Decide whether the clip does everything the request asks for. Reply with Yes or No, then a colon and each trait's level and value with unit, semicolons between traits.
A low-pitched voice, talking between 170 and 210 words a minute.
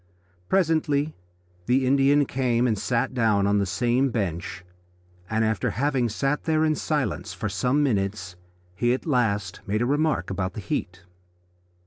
No: low, 120 Hz; average, 150 wpm